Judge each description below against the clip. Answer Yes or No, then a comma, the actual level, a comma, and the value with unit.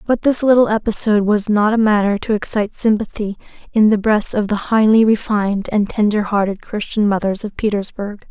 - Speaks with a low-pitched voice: No, high, 210 Hz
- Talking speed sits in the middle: Yes, average, 180 wpm